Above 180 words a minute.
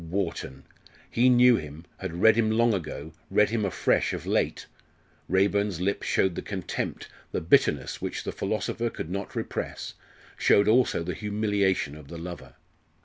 No: average, 155 wpm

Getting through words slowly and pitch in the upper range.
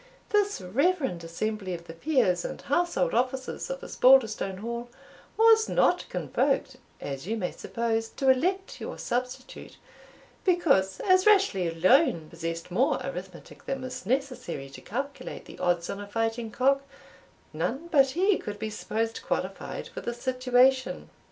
No: average, 145 wpm; very high, 250 Hz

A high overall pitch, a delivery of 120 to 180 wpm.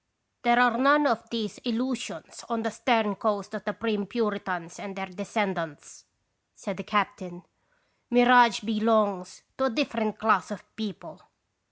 Yes: high, 215 Hz; average, 160 wpm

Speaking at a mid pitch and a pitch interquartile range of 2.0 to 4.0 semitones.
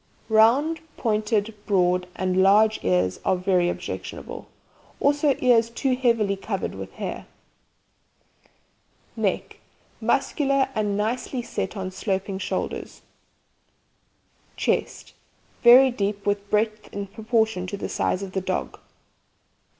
No: high, 210 Hz; average, 3.6 semitones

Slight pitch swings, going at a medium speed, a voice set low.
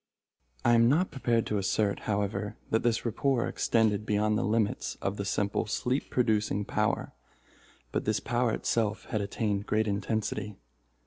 Yes: narrow, 2.2 semitones; average, 150 wpm; low, 110 Hz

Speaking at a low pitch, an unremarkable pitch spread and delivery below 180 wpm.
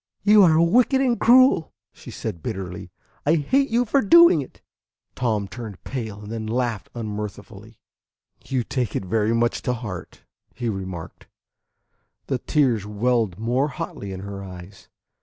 No: low, 115 Hz; wide, 6.5 semitones; average, 150 wpm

